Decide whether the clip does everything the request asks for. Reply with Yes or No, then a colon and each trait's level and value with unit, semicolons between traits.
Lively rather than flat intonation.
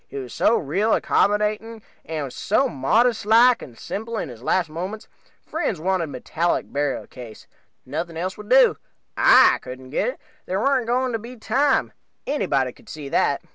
Yes: wide, 7.8 semitones